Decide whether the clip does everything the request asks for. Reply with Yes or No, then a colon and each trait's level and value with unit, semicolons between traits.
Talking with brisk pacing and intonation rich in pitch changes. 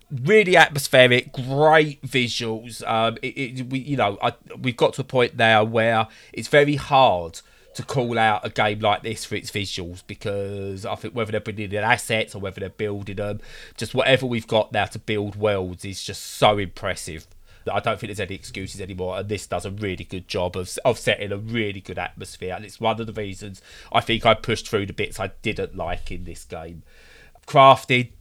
No: fast, 210 wpm; average, 4.1 semitones